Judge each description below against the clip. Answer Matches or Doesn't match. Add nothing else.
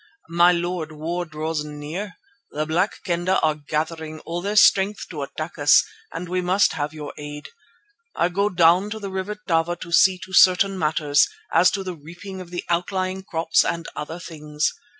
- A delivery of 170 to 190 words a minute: Matches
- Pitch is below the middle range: Doesn't match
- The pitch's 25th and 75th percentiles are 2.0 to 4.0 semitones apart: Matches